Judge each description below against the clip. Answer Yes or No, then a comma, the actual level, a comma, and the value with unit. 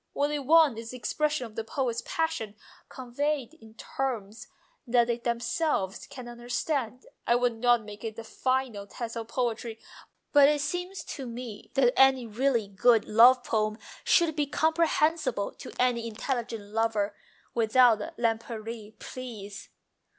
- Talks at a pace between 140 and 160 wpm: Yes, average, 145 wpm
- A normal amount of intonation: Yes, average, 3.3 semitones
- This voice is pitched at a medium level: No, high, 240 Hz